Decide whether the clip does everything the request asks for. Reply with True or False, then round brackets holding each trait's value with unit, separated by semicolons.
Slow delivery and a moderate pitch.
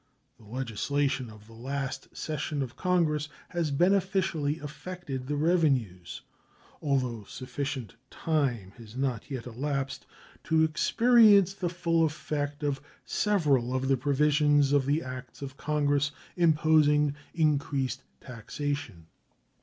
True (115 wpm; 145 Hz)